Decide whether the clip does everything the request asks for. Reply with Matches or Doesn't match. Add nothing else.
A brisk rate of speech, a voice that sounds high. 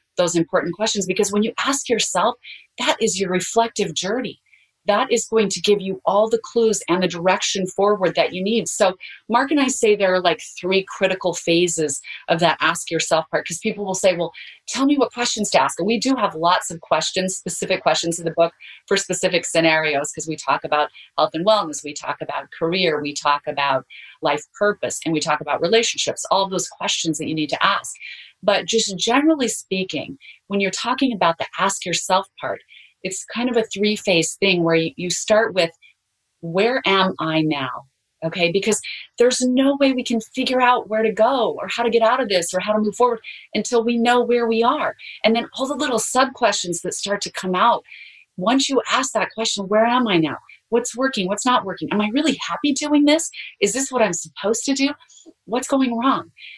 Matches